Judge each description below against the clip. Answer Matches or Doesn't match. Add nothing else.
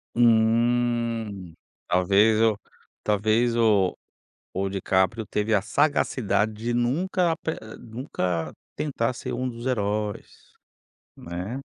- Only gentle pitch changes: Doesn't match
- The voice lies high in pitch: Doesn't match